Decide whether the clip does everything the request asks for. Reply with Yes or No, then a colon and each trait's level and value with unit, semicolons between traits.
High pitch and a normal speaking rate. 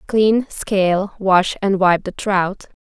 Yes: high, 195 Hz; average, 150 wpm